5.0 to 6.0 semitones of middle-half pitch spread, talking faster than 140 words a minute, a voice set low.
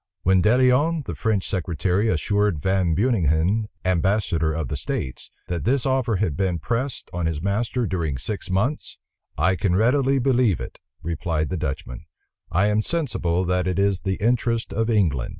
Yes: average, 5.3 semitones; average, 170 wpm; very low, 95 Hz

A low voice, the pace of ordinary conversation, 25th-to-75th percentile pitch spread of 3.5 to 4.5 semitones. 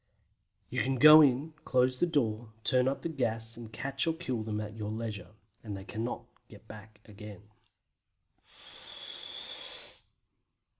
Yes: low, 115 Hz; average, 145 wpm; average, 3.8 semitones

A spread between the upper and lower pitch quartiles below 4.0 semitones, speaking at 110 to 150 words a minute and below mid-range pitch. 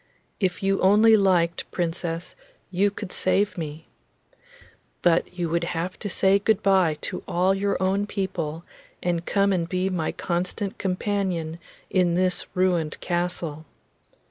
No: narrow, 2.4 semitones; average, 140 wpm; medium, 180 Hz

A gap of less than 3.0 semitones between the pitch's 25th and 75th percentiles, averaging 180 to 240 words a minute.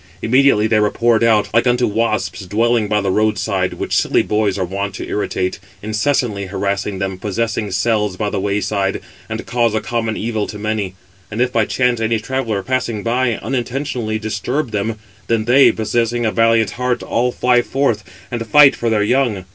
Yes: narrow, 2.5 semitones; average, 185 wpm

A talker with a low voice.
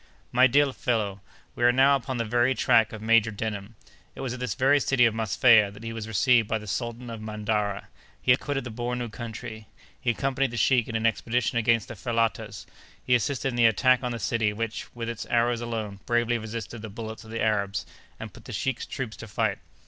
Yes: low, 115 Hz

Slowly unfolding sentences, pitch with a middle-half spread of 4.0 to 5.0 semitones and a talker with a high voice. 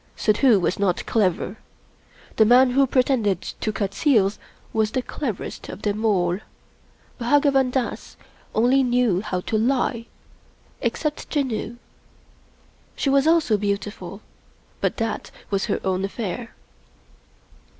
Yes: slow, 130 wpm; average, 4.5 semitones; high, 220 Hz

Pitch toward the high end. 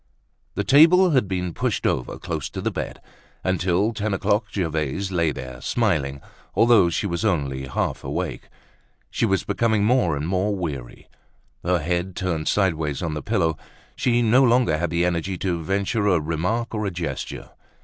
No: very low, 90 Hz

